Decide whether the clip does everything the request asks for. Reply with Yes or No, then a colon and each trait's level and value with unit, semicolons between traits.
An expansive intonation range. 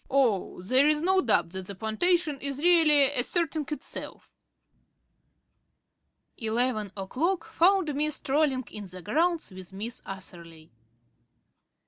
Yes: wide, 7.7 semitones